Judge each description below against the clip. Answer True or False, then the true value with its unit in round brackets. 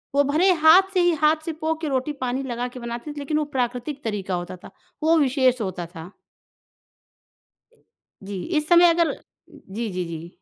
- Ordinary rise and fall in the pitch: False (7.2 semitones)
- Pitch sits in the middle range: False (260 Hz)